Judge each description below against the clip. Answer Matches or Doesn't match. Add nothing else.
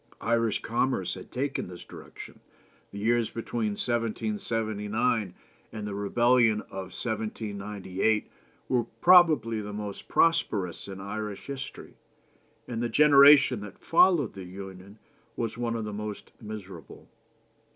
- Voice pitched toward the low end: Matches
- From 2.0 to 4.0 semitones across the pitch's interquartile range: Matches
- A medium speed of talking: Doesn't match